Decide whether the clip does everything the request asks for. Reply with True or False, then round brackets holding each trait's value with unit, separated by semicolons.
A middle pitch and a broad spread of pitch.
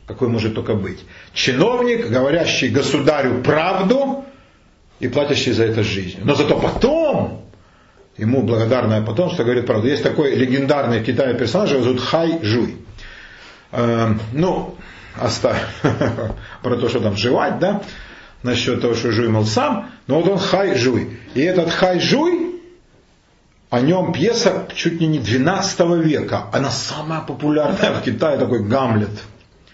False (130 Hz; 7.0 semitones)